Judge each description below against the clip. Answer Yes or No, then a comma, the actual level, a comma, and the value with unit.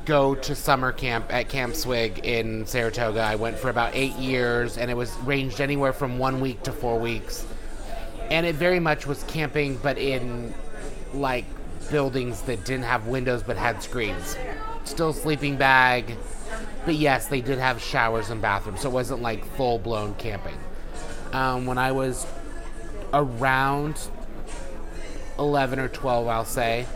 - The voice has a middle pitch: No, low, 130 Hz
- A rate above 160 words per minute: No, average, 155 wpm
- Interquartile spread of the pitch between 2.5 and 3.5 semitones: Yes, average, 2.9 semitones